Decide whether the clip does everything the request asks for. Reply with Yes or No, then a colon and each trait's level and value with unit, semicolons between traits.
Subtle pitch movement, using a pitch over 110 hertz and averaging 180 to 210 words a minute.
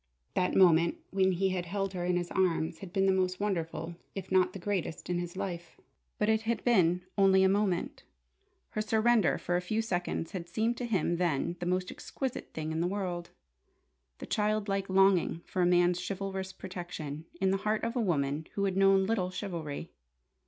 Yes: narrow, 2.2 semitones; medium, 185 Hz; average, 195 wpm